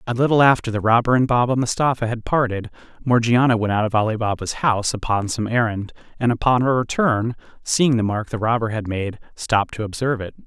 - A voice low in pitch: Yes, low, 115 Hz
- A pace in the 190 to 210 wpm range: Yes, average, 200 wpm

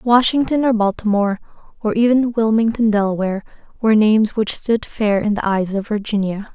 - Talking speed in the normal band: Yes, average, 155 wpm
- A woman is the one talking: Yes, female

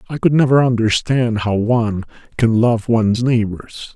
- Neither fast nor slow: Yes, average, 150 wpm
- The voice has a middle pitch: No, low, 115 Hz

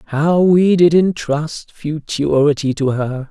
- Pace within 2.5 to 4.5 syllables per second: Yes, 3.4 syllables/s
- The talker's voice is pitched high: No, medium, 155 Hz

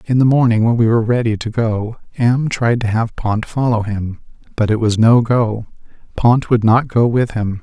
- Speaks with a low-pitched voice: Yes, low, 115 Hz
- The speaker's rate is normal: No, fast, 215 wpm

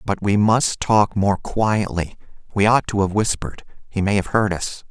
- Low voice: Yes, low, 105 Hz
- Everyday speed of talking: Yes, average, 170 wpm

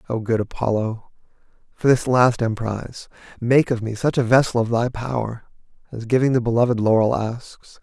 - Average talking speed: Yes, average, 170 wpm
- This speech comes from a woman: No, male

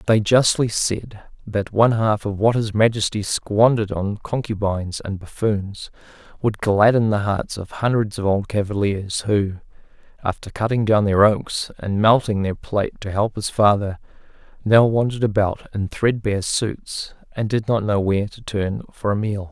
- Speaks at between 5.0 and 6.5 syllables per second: No, 4.7 syllables/s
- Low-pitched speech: Yes, low, 105 Hz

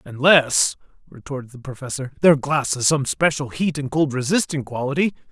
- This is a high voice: No, medium, 140 Hz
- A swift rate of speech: No, average, 160 wpm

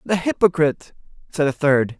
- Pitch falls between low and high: Yes, medium, 155 Hz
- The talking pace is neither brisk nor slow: Yes, average, 150 wpm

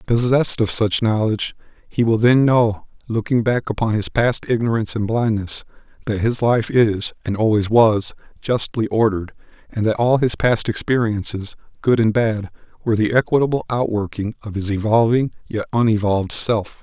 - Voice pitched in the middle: No, low, 110 Hz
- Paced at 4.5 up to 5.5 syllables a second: Yes, 5.1 syllables/s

